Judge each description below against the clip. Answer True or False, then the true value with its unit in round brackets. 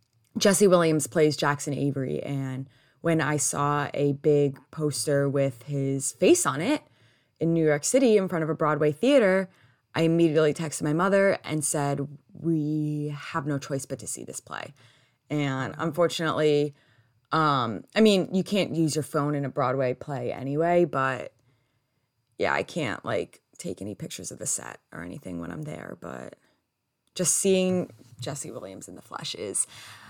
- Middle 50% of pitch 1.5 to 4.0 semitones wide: True (3.5 semitones)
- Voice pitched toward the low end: False (145 Hz)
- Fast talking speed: False (165 wpm)